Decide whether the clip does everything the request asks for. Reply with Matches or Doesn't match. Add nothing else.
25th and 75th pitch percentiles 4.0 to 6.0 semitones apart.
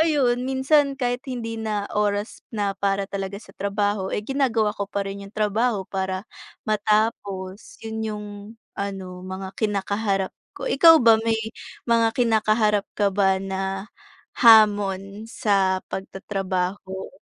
Doesn't match